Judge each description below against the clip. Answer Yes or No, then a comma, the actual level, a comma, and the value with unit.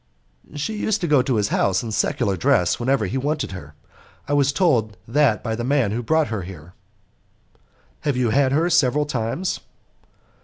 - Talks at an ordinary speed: Yes, average, 180 wpm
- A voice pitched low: Yes, low, 125 Hz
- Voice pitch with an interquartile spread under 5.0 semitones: No, average, 5.3 semitones